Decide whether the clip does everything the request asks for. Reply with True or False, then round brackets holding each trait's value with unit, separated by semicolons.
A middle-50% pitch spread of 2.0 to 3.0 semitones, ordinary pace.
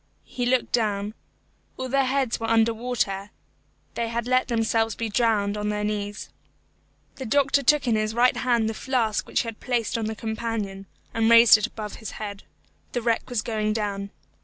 True (2.4 semitones; 185 wpm)